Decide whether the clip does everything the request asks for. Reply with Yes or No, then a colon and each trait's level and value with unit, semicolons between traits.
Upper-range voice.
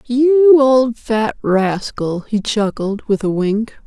Yes: high, 230 Hz